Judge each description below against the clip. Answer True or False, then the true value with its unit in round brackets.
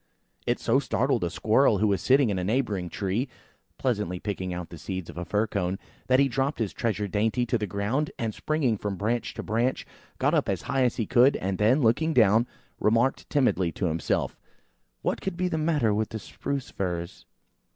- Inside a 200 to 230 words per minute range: True (205 wpm)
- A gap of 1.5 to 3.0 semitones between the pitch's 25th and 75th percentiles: False (5.0 semitones)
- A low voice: True (110 Hz)